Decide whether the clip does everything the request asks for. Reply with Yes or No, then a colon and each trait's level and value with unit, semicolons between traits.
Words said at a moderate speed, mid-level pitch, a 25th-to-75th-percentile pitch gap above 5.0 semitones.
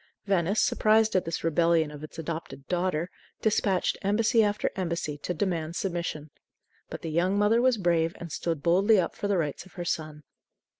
No: average, 180 wpm; medium, 175 Hz; average, 3.8 semitones